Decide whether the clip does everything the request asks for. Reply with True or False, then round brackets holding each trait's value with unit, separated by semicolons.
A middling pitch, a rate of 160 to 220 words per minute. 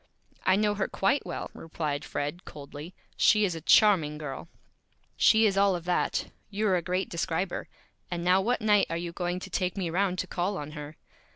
True (180 Hz; 195 wpm)